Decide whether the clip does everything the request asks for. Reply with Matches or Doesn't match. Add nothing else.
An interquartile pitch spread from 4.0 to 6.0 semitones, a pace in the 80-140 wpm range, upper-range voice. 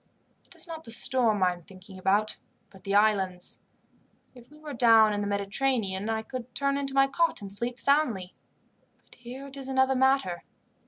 Doesn't match